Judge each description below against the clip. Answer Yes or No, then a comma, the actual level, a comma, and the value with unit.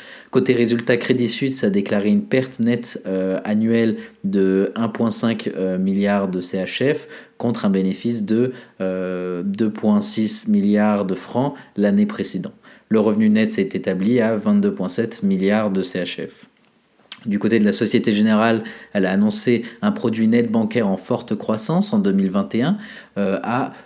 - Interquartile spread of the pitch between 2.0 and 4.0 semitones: Yes, average, 3.2 semitones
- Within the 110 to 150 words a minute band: Yes, slow, 145 wpm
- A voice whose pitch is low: Yes, low, 110 Hz